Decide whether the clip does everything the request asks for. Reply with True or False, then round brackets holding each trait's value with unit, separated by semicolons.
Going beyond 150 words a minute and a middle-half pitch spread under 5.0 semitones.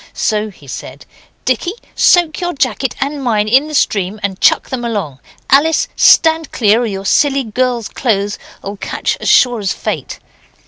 False (165 wpm; 5.3 semitones)